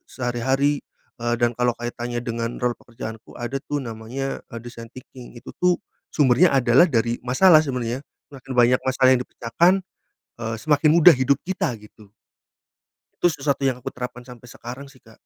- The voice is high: No, low, 125 Hz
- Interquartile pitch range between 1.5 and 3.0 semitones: Yes, narrow, 2.6 semitones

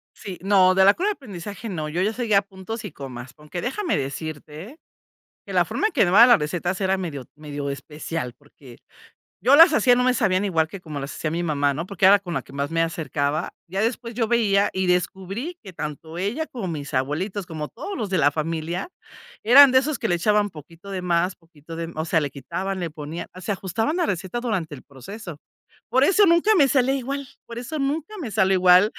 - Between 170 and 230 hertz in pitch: Yes, medium, 185 Hz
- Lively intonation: Yes, wide, 6.6 semitones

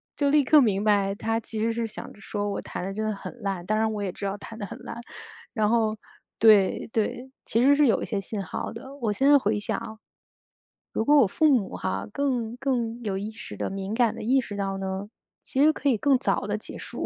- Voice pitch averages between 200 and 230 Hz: Yes, high, 220 Hz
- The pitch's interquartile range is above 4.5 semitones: No, average, 3.5 semitones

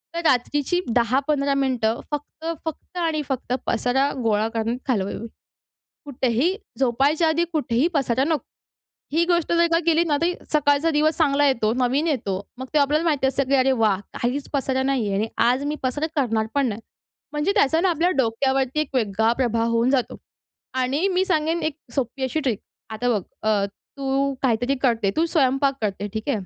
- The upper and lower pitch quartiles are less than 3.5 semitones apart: No, average, 4.2 semitones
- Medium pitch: No, very high, 270 Hz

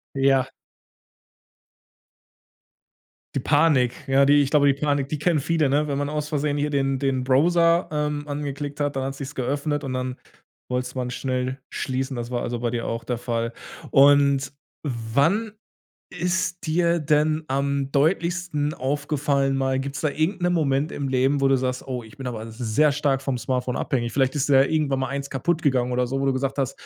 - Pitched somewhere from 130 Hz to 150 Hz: Yes, medium, 140 Hz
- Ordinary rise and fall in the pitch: No, narrow, 2.3 semitones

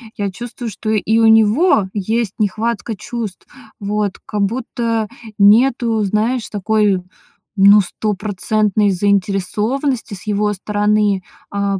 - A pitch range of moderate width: No, narrow, 2.0 semitones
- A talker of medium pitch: No, high, 210 Hz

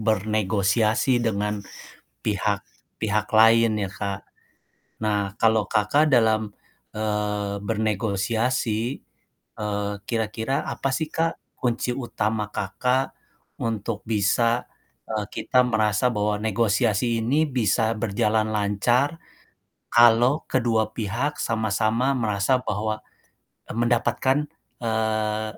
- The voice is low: Yes, low, 110 Hz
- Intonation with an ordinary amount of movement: No, narrow, 2.3 semitones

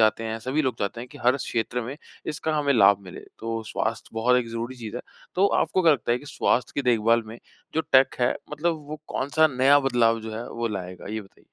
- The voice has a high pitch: No, low, 120 Hz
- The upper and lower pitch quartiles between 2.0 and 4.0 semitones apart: Yes, average, 3.7 semitones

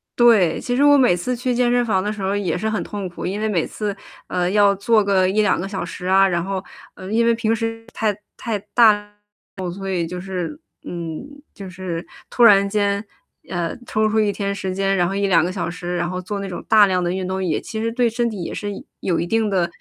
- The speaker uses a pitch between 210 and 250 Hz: No, high, 200 Hz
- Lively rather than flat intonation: No, average, 3.0 semitones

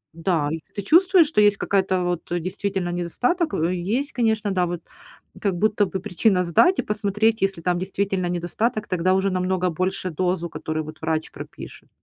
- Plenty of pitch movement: No, average, 3.1 semitones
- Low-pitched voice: No, medium, 185 Hz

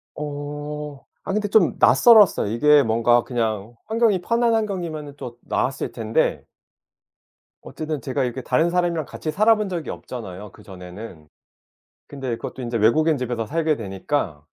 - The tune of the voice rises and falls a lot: Yes, wide, 6.5 semitones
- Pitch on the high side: No, medium, 145 Hz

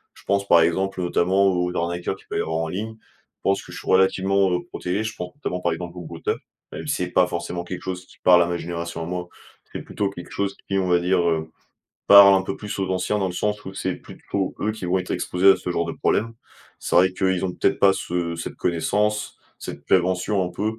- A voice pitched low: Yes, very low, 90 Hz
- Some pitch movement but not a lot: No, narrow, 2.0 semitones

